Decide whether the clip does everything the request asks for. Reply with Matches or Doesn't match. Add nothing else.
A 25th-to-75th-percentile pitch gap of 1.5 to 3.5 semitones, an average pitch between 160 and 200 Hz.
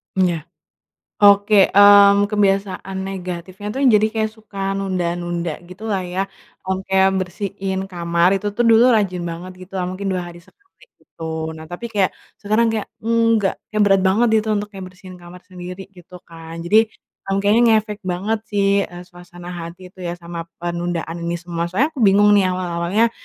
Matches